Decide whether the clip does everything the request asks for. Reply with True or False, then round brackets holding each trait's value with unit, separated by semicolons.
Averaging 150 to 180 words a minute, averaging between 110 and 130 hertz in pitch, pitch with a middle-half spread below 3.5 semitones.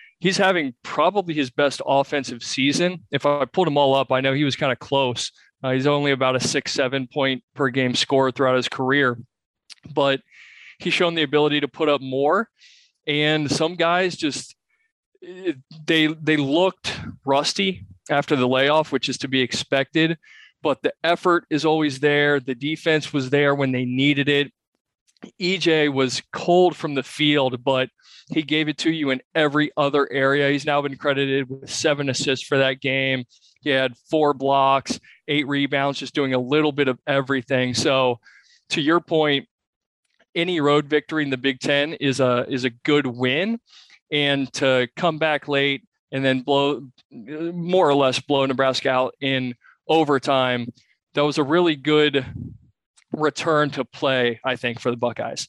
False (170 wpm; 140 Hz; 2.6 semitones)